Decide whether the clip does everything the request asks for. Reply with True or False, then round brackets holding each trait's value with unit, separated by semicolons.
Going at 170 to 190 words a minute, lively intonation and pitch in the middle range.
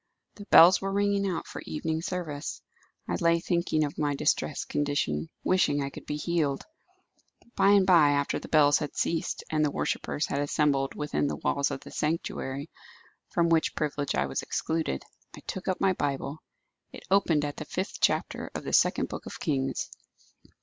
False (180 wpm; 3.2 semitones; 150 Hz)